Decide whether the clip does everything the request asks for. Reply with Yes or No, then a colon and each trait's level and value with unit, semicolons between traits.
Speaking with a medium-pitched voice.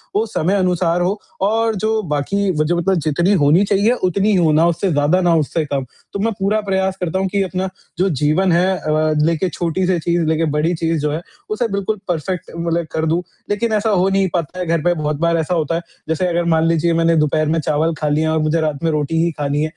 Yes: medium, 170 Hz